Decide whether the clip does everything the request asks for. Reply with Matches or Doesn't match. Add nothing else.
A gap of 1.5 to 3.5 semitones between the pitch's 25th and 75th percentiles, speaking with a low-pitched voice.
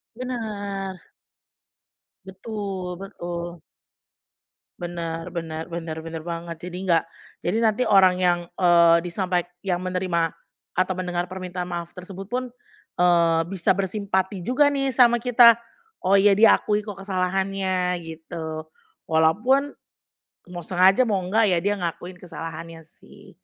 Doesn't match